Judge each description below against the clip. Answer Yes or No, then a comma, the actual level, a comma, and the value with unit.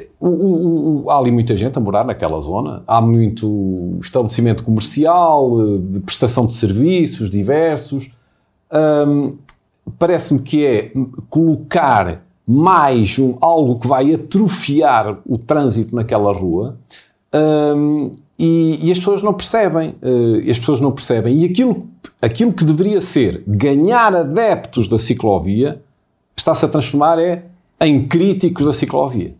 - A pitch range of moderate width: No, wide, 6.0 semitones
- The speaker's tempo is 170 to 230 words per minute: No, average, 125 wpm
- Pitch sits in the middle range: Yes, medium, 145 Hz